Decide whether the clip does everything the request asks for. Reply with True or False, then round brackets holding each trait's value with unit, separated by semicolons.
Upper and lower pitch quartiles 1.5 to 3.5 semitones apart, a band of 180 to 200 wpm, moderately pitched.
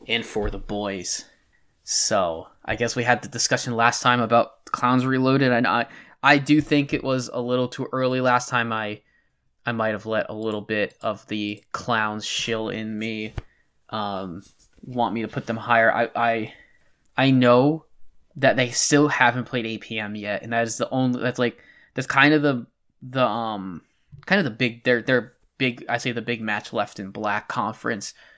False (2.7 semitones; 190 wpm; 120 Hz)